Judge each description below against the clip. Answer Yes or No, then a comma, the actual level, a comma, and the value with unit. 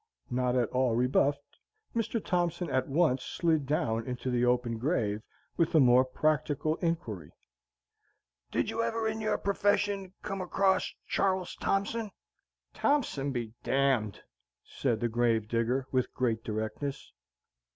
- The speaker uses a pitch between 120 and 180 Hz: Yes, low, 135 Hz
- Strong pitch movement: Yes, wide, 6.8 semitones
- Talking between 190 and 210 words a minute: No, average, 140 wpm